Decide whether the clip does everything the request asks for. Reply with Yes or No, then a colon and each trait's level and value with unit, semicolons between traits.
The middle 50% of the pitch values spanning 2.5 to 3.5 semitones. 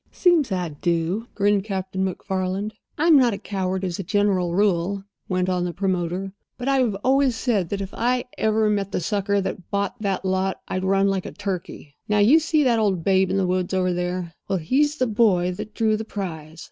Yes: average, 2.8 semitones